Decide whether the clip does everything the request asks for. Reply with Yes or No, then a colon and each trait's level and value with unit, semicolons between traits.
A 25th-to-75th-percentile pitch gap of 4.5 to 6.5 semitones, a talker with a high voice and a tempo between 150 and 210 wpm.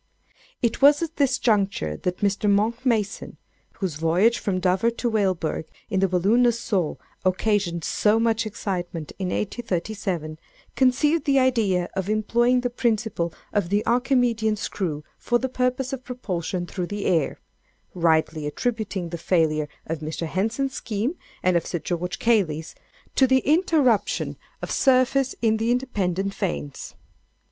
No: wide, 5.4 semitones; high, 210 Hz; average, 140 wpm